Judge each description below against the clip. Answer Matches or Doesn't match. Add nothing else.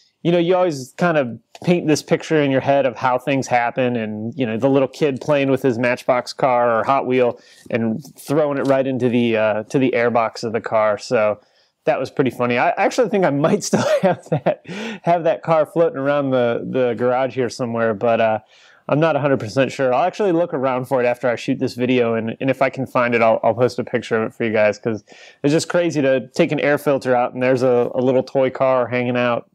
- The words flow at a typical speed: Doesn't match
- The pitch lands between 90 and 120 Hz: Doesn't match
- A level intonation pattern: Doesn't match